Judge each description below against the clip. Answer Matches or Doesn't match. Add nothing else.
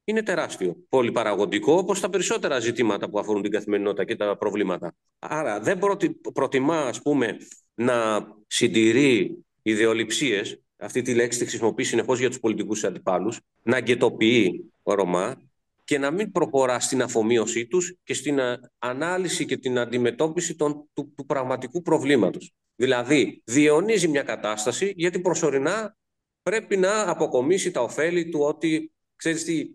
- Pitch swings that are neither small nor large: Doesn't match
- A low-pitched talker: Doesn't match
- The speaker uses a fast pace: Doesn't match